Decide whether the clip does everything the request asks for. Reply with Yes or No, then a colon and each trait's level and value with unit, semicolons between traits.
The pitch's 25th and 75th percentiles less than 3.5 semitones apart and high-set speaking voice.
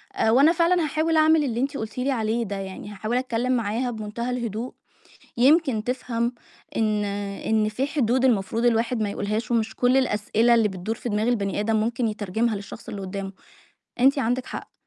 Yes: average, 3.1 semitones; high, 230 Hz